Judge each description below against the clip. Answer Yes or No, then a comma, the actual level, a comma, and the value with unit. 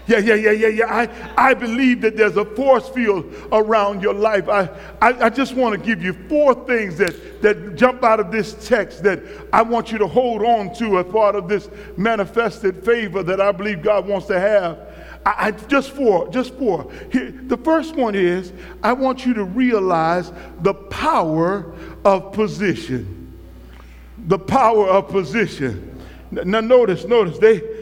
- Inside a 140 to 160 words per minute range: No, average, 180 wpm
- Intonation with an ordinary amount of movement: Yes, average, 3.3 semitones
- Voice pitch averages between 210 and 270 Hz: Yes, high, 215 Hz